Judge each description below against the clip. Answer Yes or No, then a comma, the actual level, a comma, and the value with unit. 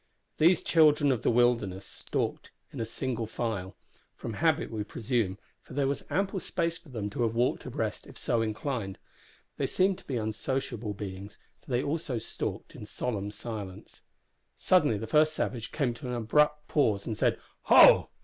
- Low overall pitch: Yes, low, 120 Hz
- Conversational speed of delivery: Yes, average, 170 wpm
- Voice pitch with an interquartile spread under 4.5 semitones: No, average, 5.3 semitones